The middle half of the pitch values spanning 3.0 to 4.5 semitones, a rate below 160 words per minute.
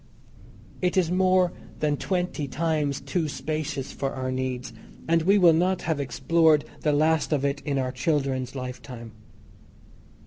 Yes: average, 3.8 semitones; average, 145 wpm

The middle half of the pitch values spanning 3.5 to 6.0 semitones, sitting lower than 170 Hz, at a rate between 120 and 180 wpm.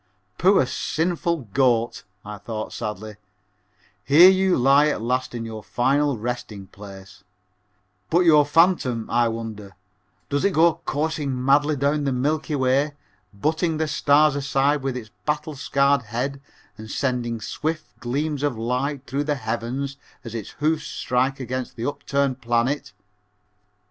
Yes: average, 4.0 semitones; low, 135 Hz; average, 140 wpm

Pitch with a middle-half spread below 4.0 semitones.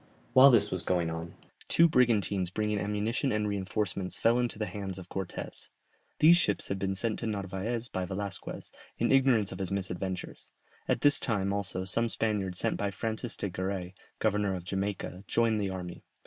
Yes: average, 2.9 semitones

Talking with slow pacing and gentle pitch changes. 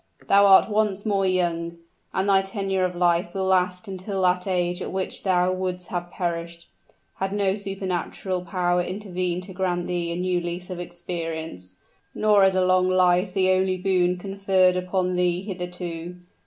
No: average, 170 wpm; narrow, 1.4 semitones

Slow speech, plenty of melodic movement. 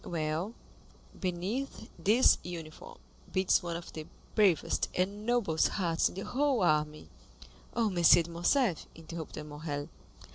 No: slow, 130 wpm; average, 4.5 semitones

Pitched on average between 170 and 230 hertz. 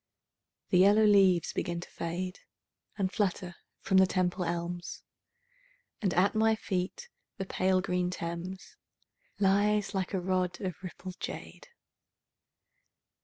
Yes: medium, 185 Hz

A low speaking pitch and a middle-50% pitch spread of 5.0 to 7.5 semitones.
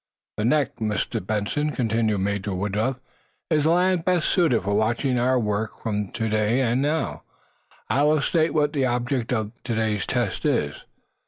Yes: low, 120 Hz; wide, 5.6 semitones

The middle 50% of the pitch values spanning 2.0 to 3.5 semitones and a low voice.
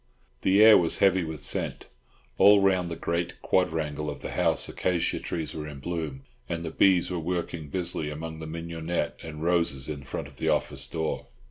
Yes: narrow, 2.5 semitones; very low, 80 Hz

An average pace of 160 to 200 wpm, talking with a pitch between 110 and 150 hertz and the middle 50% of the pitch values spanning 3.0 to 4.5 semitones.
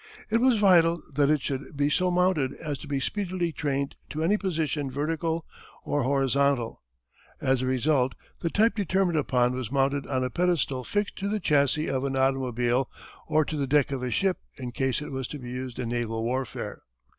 Yes: average, 195 wpm; medium, 140 Hz; average, 4.2 semitones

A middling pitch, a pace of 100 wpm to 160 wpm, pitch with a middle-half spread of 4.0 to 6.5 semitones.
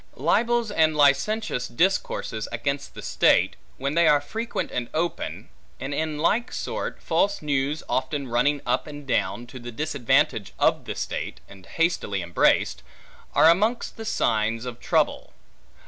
Yes: medium, 145 Hz; average, 145 wpm; wide, 5.4 semitones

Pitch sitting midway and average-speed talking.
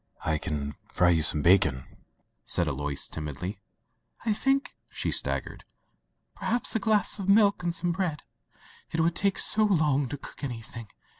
Yes: medium, 145 Hz; average, 160 wpm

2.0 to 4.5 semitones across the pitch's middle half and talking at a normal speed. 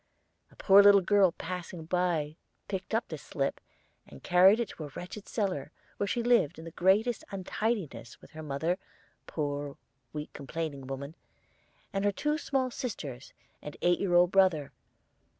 No: average, 5.2 semitones; average, 165 wpm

